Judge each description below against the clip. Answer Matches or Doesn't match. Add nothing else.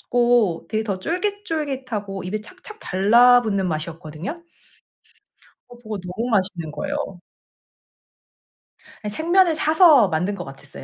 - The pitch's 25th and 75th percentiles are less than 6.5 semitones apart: Doesn't match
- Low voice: Doesn't match